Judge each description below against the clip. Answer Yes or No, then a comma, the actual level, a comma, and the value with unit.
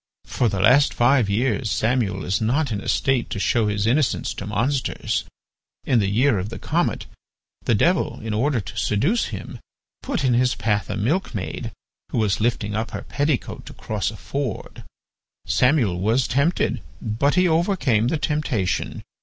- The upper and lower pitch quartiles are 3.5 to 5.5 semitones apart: Yes, average, 5.2 semitones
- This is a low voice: Yes, low, 120 Hz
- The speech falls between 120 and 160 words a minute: No, average, 170 wpm